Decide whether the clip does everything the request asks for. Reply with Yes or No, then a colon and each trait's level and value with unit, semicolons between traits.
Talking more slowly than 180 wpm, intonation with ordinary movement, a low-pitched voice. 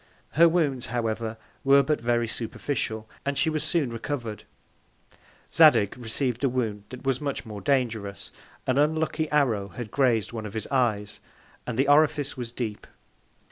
Yes: average, 155 wpm; average, 4.1 semitones; low, 125 Hz